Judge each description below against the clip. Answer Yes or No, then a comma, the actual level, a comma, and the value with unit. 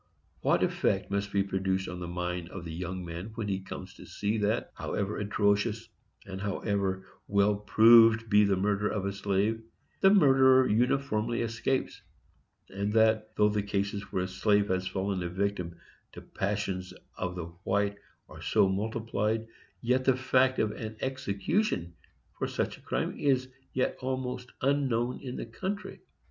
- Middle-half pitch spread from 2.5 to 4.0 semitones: Yes, average, 3.3 semitones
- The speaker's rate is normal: Yes, average, 160 wpm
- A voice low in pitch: Yes, low, 105 Hz